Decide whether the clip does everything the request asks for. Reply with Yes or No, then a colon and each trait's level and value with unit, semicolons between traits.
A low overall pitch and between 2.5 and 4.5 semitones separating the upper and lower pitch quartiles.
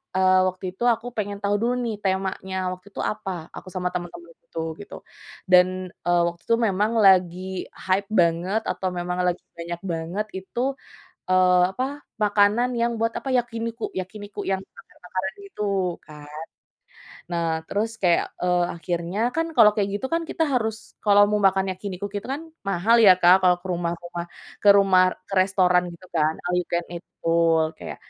No: medium, 185 Hz; average, 2.8 semitones